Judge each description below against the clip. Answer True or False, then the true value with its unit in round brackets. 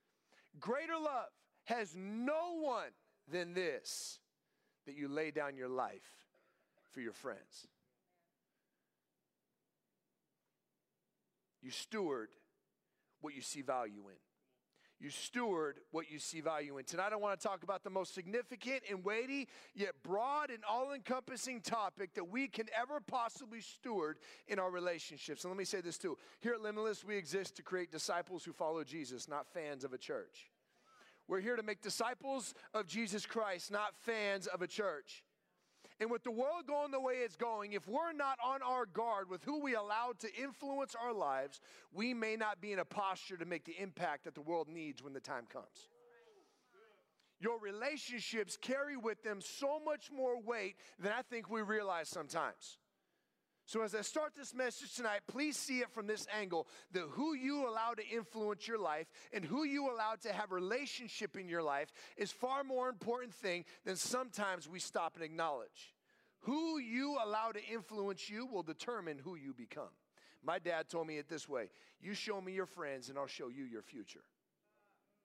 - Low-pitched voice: False (215 Hz)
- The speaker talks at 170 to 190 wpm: True (175 wpm)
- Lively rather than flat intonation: True (5.8 semitones)